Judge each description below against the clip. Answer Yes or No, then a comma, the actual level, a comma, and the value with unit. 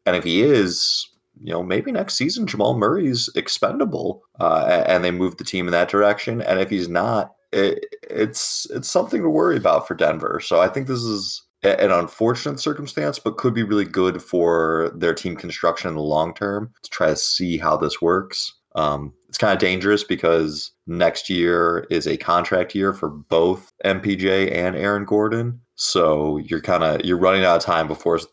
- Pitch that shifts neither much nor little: Yes, average, 3.9 semitones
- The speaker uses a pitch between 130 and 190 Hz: No, very low, 95 Hz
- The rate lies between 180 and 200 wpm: Yes, average, 190 wpm